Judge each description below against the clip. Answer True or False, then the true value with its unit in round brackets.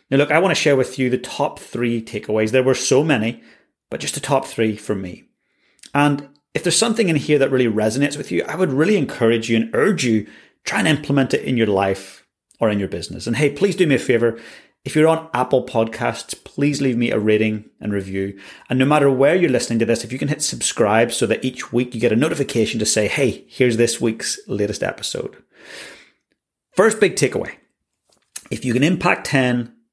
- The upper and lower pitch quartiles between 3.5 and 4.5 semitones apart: True (4.2 semitones)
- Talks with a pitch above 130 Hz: False (125 Hz)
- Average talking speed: False (220 wpm)